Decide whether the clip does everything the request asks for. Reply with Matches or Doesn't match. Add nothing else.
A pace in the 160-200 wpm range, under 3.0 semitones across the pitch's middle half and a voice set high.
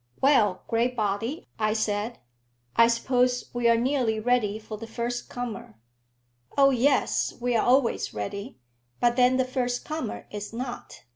Doesn't match